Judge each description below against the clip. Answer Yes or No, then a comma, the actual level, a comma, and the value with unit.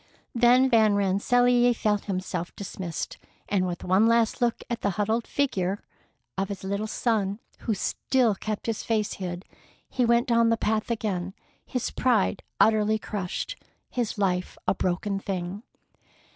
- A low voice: No, high, 210 Hz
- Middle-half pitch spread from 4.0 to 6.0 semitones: No, average, 3.3 semitones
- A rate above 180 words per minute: No, average, 145 wpm